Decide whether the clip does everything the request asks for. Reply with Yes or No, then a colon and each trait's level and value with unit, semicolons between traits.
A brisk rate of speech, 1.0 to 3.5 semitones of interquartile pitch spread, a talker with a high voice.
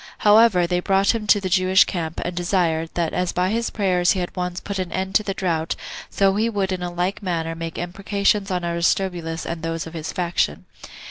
No: fast, 210 wpm; narrow, 2.4 semitones; medium, 180 Hz